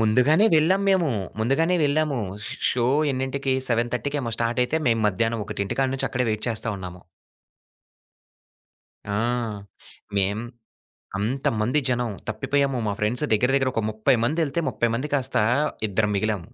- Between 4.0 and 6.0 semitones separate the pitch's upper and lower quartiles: Yes, average, 4.4 semitones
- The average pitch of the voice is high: No, low, 125 Hz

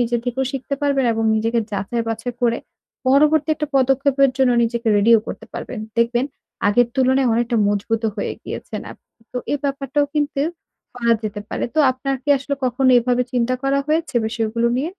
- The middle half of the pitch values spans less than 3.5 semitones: Yes, average, 2.9 semitones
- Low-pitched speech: No, very high, 250 Hz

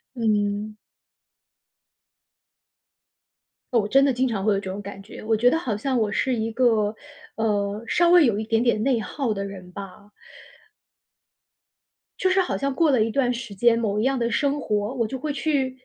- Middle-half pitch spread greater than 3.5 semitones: Yes, average, 4.0 semitones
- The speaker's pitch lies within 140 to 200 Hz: No, high, 225 Hz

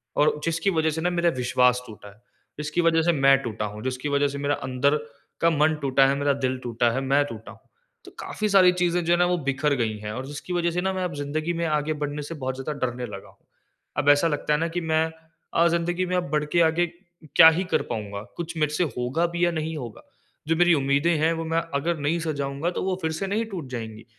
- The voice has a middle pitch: Yes, medium, 150 Hz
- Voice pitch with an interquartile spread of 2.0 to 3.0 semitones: No, average, 4.0 semitones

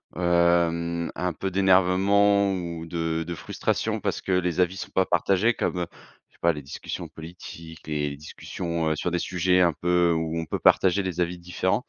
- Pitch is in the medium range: No, very low, 85 Hz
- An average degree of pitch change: No, narrow, 1.8 semitones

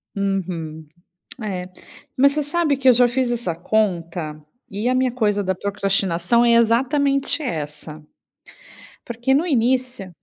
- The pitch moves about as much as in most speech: No, wide, 6.1 semitones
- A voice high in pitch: Yes, high, 220 Hz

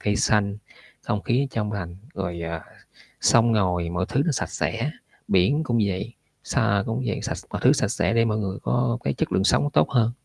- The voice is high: No, low, 105 Hz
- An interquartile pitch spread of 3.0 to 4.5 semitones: Yes, average, 4.0 semitones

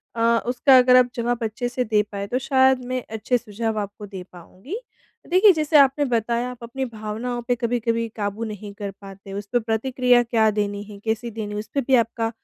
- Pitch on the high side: Yes, high, 230 Hz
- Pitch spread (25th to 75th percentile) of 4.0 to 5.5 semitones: No, average, 3.0 semitones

